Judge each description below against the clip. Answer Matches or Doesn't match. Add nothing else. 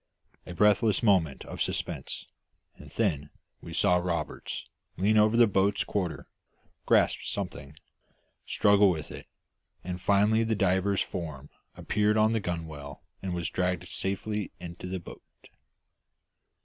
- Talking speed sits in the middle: Doesn't match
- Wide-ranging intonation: Doesn't match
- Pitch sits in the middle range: Doesn't match